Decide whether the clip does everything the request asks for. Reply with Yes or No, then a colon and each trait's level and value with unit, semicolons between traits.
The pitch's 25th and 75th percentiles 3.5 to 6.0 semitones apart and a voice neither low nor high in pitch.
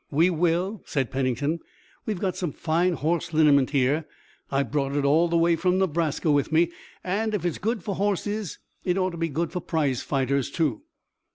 Yes: average, 3.9 semitones; medium, 165 Hz